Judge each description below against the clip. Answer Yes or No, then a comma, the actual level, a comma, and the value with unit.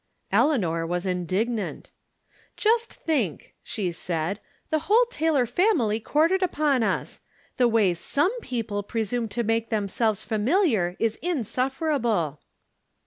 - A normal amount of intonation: No, wide, 7.1 semitones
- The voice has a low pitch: No, high, 230 Hz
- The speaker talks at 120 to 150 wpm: Yes, slow, 135 wpm